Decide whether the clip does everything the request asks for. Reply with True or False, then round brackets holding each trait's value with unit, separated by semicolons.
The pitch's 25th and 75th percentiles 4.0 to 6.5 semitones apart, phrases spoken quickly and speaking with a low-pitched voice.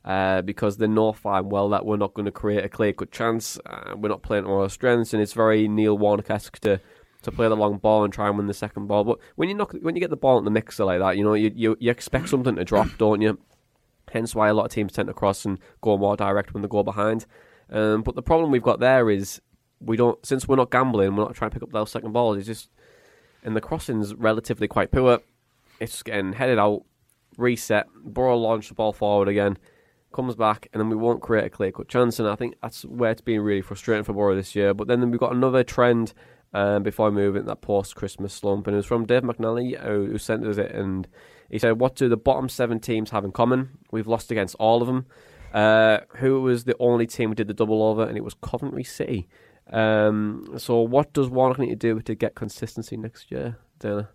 False (2.7 semitones; 245 wpm; 110 Hz)